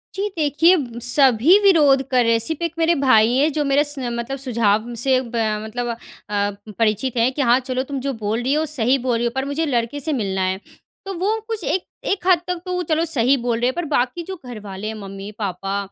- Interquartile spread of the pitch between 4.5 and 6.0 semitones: Yes, average, 5.1 semitones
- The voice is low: No, very high, 260 Hz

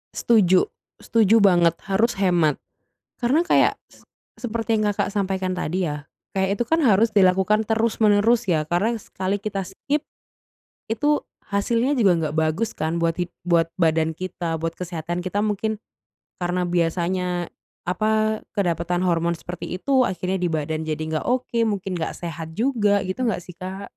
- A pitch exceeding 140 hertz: Yes, medium, 185 Hz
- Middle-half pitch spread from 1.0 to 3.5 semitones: No, average, 4.1 semitones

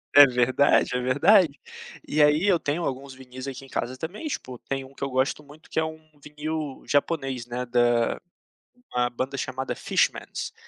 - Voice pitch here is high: No, low, 135 Hz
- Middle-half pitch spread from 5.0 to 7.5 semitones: No, average, 3.0 semitones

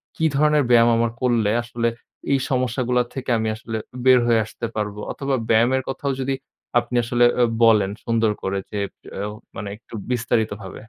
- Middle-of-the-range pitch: No, low, 120 Hz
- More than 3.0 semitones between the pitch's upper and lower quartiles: No, narrow, 2.5 semitones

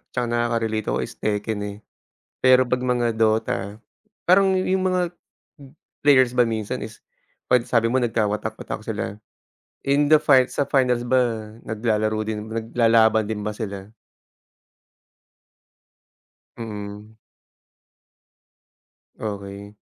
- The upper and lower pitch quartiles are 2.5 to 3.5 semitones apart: Yes, average, 2.9 semitones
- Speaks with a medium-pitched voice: No, low, 115 Hz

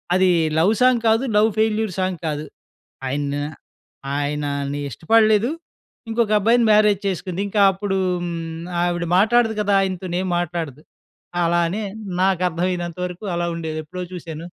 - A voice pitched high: No, medium, 180 Hz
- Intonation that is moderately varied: Yes, average, 4.2 semitones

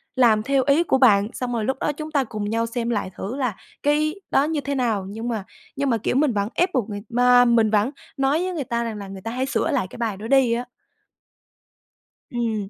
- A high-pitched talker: Yes, high, 240 Hz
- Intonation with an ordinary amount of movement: Yes, average, 4.0 semitones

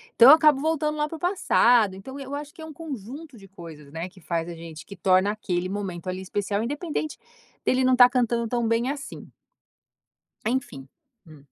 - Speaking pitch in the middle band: No, high, 230 Hz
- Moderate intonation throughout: No, wide, 7.5 semitones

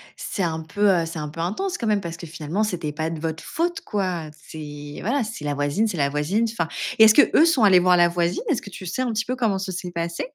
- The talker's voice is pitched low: No, medium, 180 Hz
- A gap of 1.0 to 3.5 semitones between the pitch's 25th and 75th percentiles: No, average, 5.0 semitones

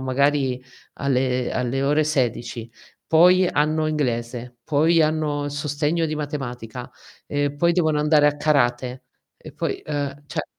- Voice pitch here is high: No, medium, 145 Hz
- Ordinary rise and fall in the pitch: Yes, average, 3.2 semitones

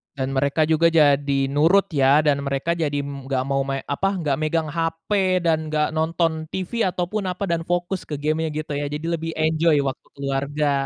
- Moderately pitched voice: Yes, medium, 155 Hz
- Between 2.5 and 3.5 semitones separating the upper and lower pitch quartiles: Yes, average, 2.8 semitones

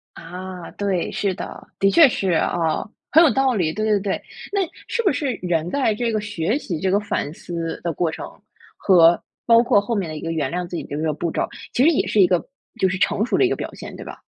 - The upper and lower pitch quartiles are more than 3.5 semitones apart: Yes, average, 4.5 semitones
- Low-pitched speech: No, high, 190 Hz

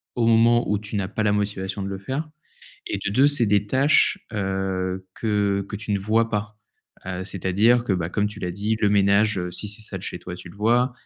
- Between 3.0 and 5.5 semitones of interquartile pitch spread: No, narrow, 2.5 semitones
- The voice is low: Yes, low, 105 Hz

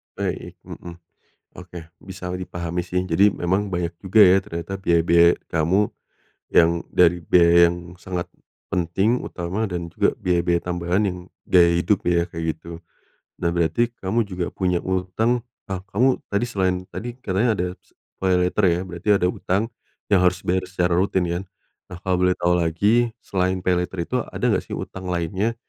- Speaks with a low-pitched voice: Yes, very low, 90 Hz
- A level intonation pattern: Yes, narrow, 1.9 semitones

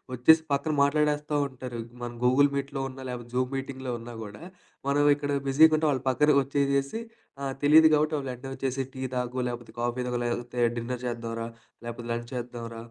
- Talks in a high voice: No, low, 130 Hz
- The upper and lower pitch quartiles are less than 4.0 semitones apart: Yes, average, 2.9 semitones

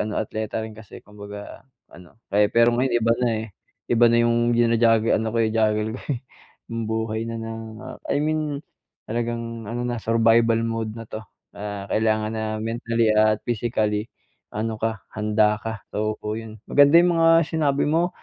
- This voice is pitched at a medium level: No, low, 115 Hz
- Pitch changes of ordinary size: No, narrow, 1.5 semitones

